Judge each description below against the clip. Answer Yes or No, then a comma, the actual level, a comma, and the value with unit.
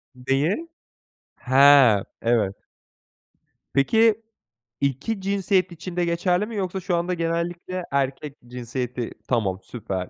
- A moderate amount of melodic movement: No, wide, 6.5 semitones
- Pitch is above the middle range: No, medium, 155 Hz